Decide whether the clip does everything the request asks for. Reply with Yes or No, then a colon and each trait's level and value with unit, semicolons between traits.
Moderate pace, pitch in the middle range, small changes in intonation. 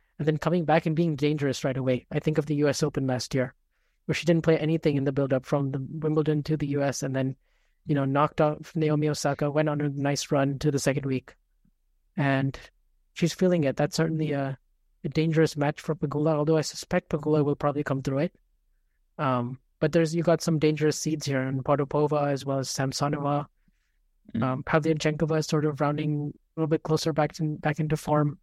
No: fast, 210 wpm; medium, 150 Hz; narrow, 2.2 semitones